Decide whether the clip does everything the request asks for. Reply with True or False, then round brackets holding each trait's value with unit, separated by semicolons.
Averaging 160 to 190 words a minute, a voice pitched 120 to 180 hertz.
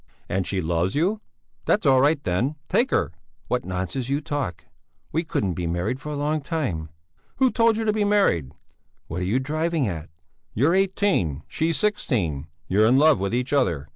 True (185 wpm; 135 Hz)